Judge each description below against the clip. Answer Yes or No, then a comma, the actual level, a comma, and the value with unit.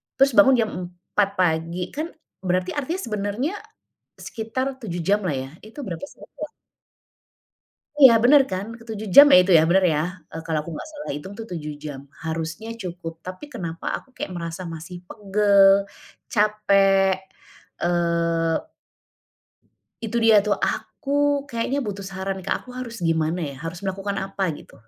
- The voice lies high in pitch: Yes, high, 195 Hz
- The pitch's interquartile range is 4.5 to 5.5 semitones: Yes, average, 5.1 semitones